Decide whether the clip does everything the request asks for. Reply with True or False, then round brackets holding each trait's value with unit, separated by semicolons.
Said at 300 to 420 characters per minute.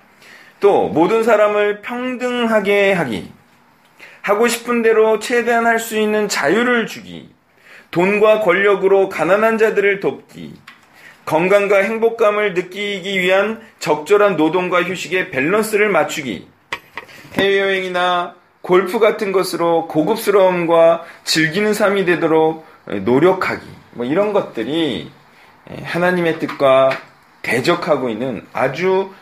False (255 characters per minute)